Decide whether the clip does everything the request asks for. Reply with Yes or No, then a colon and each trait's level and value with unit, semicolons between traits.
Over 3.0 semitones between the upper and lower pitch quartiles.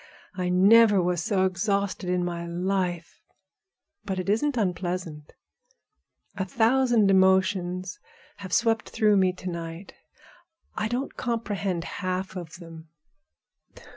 No: average, 2.7 semitones